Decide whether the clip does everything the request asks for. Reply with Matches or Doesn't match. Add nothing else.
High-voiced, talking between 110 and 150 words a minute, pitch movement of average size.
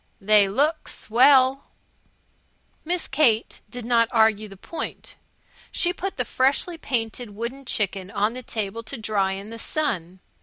Matches